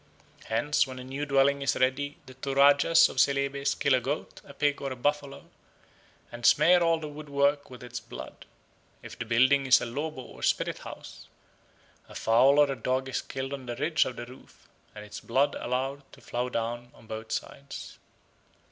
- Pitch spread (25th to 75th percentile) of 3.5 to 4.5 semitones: No, narrow, 2.4 semitones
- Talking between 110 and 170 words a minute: No, average, 190 wpm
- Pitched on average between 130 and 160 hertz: Yes, low, 135 Hz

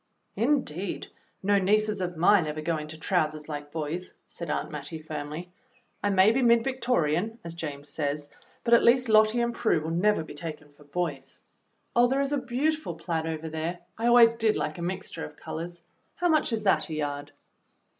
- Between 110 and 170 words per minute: No, average, 190 wpm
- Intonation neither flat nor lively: No, wide, 6.7 semitones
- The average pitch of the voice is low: No, medium, 175 Hz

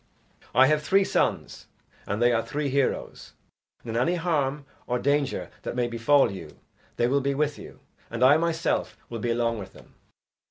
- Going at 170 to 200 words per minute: Yes, average, 185 wpm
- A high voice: No, low, 135 Hz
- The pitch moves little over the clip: No, average, 4.0 semitones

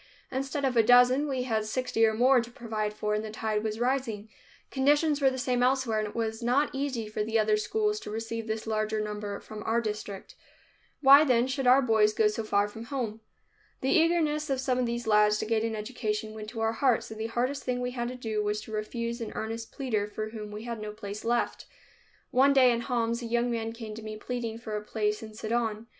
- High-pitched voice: Yes, high, 230 Hz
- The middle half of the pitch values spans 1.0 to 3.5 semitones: Yes, average, 2.8 semitones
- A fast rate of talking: Yes, fast, 235 wpm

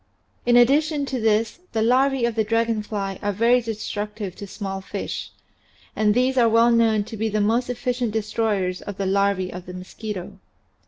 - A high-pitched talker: Yes, high, 220 Hz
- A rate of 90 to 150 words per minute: No, average, 180 wpm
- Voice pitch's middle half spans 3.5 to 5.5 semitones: No, average, 2.8 semitones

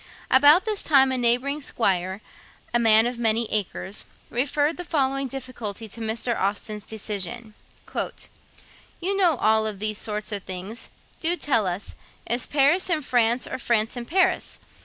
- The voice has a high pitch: Yes, high, 235 Hz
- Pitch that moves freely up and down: No, average, 4.3 semitones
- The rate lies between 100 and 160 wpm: Yes, average, 155 wpm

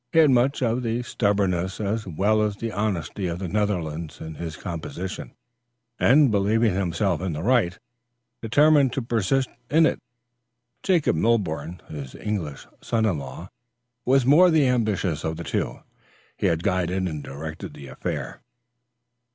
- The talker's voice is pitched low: Yes, low, 100 Hz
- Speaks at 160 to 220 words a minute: No, average, 150 wpm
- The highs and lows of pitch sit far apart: Yes, wide, 5.8 semitones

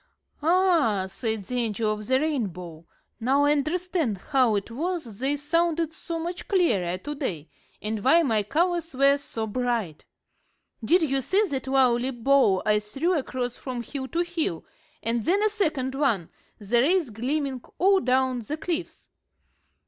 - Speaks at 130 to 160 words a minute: Yes, average, 155 wpm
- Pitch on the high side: Yes, very high, 265 Hz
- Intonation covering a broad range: Yes, wide, 6.6 semitones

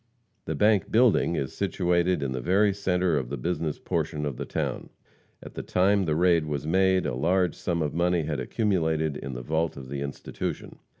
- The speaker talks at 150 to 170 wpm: No, average, 195 wpm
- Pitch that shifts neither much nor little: Yes, average, 3.9 semitones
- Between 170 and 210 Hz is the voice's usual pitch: No, very low, 85 Hz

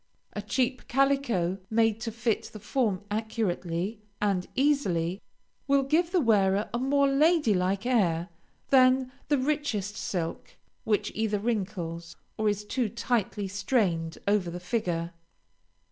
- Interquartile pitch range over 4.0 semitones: Yes, wide, 5.4 semitones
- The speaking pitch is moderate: No, high, 215 Hz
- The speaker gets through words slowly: Yes, slow, 130 wpm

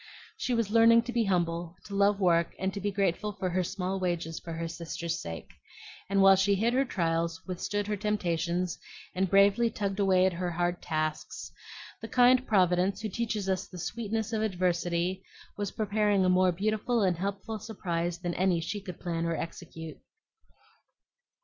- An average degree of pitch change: Yes, average, 3.2 semitones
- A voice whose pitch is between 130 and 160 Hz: No, high, 190 Hz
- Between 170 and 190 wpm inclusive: Yes, average, 175 wpm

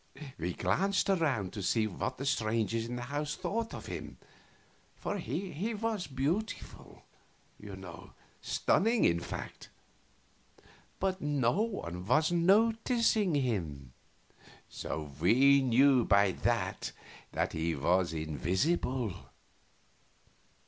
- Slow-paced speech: Yes, slow, 110 wpm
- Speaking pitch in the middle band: No, low, 130 Hz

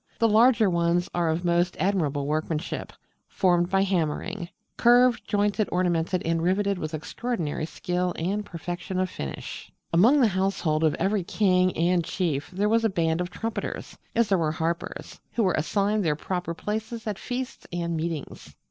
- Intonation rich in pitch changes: No, average, 3.7 semitones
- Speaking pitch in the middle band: Yes, medium, 180 Hz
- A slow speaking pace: No, average, 165 wpm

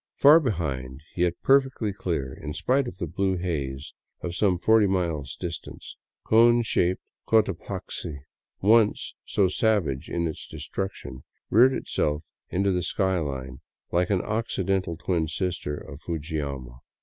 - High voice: No, very low, 90 Hz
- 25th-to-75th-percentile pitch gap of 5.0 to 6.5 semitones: Yes, wide, 5.5 semitones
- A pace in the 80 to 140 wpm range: Yes, slow, 135 wpm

